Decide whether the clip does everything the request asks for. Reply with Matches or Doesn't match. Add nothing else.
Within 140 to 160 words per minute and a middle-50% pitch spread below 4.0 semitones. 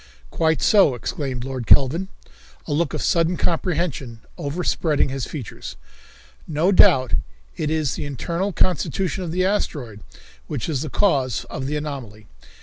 Doesn't match